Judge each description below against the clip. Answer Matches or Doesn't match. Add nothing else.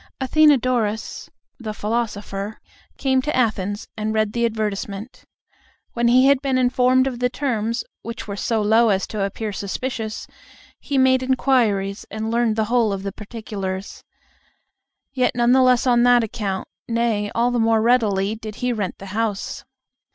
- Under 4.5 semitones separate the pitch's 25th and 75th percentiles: Matches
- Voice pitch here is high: Matches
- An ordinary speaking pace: Matches